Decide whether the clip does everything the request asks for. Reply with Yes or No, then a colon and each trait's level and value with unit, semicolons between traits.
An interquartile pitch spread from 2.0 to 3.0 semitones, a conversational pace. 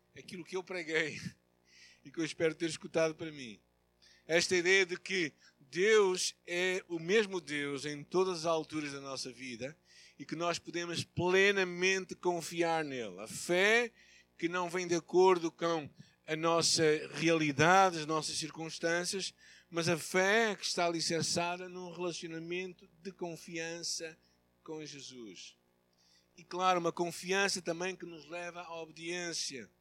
Yes: narrow, 2.6 semitones; average, 145 wpm